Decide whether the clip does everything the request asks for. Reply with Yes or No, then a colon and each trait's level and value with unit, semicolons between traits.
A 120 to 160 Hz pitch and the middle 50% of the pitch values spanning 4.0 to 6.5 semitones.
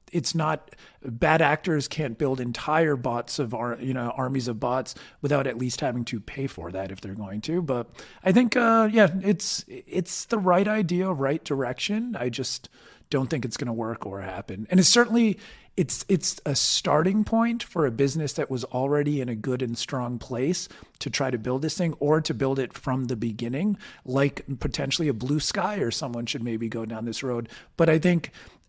Yes: medium, 140 Hz; wide, 5.5 semitones